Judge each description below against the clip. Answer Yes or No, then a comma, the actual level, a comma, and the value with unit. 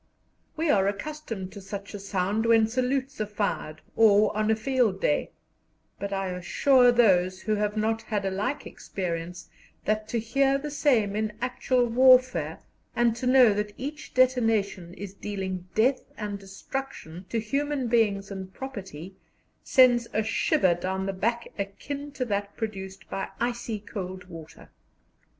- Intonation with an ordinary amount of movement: Yes, average, 4.3 semitones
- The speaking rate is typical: Yes, average, 155 wpm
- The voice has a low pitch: No, high, 215 Hz